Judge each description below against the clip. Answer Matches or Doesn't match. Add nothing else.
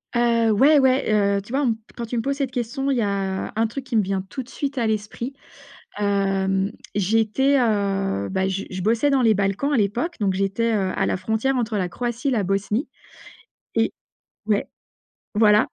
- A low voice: Doesn't match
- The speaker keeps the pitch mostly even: Doesn't match